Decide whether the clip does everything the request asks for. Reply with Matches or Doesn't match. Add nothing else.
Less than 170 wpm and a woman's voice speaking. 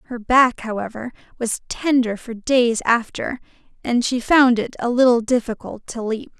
Matches